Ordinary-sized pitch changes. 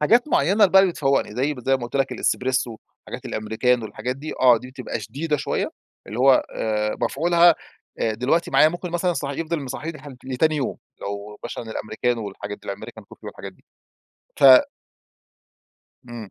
No: wide, 5.7 semitones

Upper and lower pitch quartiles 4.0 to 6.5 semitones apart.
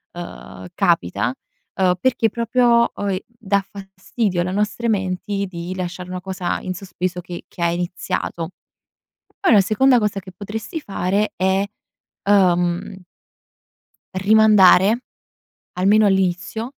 No: average, 2.9 semitones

